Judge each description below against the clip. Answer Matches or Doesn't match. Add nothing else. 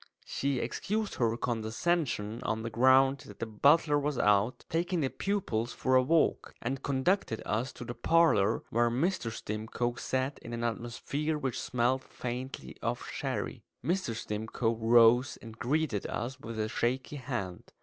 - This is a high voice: Doesn't match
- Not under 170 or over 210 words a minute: Doesn't match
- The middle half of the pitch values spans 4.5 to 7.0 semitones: Doesn't match